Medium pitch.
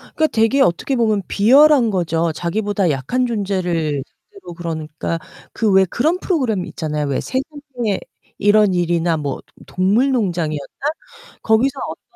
No: high, 200 Hz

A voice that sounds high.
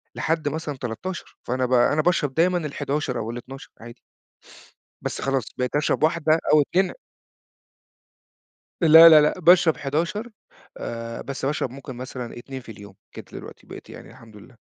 No: medium, 140 Hz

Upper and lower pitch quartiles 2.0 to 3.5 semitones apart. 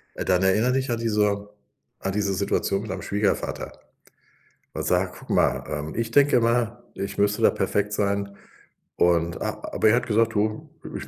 Yes: average, 2.7 semitones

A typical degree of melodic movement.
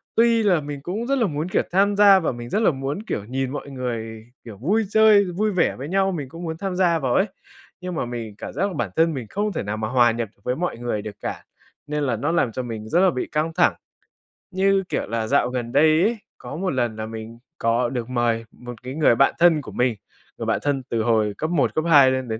No: wide, 7.2 semitones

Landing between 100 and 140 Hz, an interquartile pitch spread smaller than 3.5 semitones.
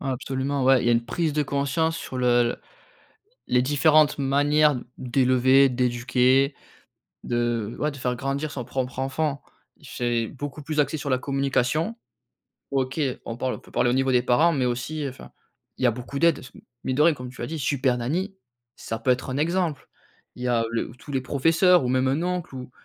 Yes: low, 135 Hz; average, 3.0 semitones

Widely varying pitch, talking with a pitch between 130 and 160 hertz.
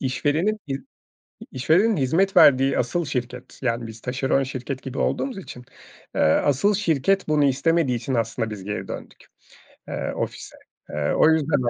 No: average, 4.5 semitones; low, 135 Hz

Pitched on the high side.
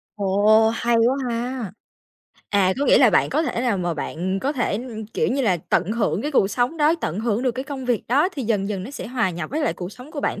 Yes: high, 230 Hz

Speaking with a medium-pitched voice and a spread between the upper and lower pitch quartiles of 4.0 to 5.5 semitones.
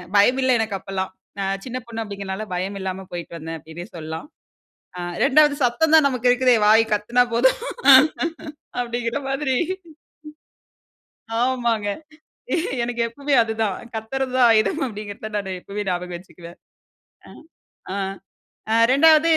No: high, 225 Hz; average, 4.7 semitones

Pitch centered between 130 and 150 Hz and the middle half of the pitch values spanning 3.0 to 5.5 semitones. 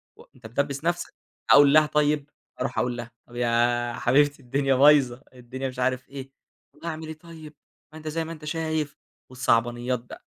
Yes: medium, 140 Hz; average, 3.8 semitones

